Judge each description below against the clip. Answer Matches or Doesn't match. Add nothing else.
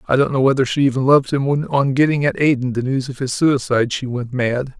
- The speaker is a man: Matches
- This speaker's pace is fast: Matches